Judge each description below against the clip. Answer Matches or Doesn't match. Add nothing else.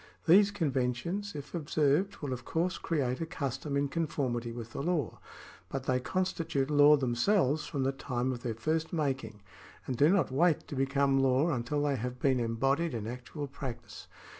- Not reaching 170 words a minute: Doesn't match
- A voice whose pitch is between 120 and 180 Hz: Matches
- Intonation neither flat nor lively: Matches